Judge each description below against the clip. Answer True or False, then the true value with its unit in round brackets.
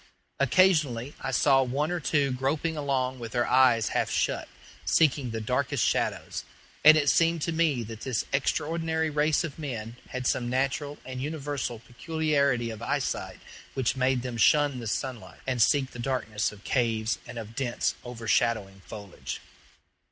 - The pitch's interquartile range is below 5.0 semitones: True (4.0 semitones)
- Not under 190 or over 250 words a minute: False (160 wpm)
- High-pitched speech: False (130 Hz)